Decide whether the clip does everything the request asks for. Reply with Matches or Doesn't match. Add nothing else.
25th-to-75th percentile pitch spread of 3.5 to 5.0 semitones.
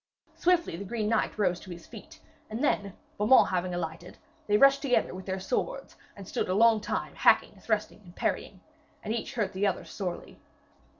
Matches